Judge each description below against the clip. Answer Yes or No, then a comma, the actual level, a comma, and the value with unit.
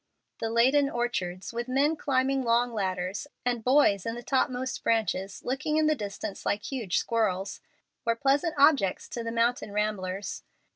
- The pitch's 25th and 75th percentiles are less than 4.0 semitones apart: No, average, 4.4 semitones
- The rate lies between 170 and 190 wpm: No, average, 155 wpm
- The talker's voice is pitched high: Yes, high, 235 Hz